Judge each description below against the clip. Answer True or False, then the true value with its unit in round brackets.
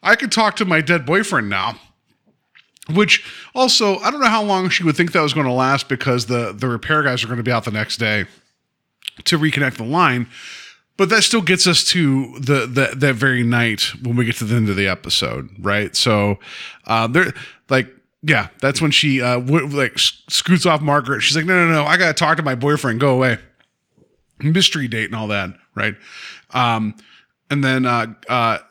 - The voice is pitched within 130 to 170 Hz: True (140 Hz)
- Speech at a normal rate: False (210 wpm)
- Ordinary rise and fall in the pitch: False (5.7 semitones)